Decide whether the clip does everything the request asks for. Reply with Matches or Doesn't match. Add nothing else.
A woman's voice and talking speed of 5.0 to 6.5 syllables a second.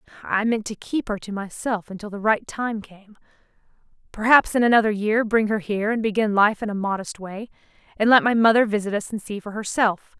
Matches